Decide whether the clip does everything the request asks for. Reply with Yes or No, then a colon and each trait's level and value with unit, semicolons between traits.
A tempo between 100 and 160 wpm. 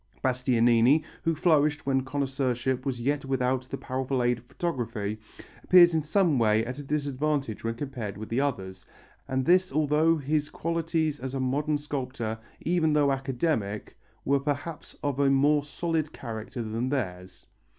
Yes: average, 155 wpm